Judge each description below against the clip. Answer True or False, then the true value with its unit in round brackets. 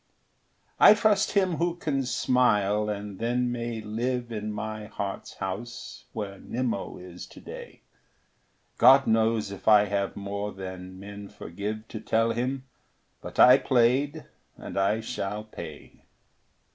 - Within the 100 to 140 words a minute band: True (135 wpm)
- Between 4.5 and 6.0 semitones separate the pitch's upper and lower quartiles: False (3.6 semitones)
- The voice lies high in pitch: False (110 Hz)